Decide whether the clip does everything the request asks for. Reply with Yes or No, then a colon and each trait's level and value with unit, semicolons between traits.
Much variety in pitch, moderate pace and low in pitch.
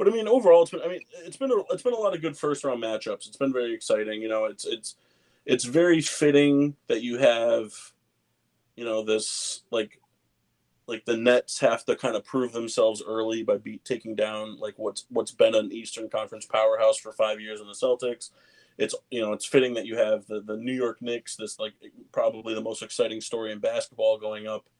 No: wide, 7.3 semitones; fast, 210 wpm; low, 120 Hz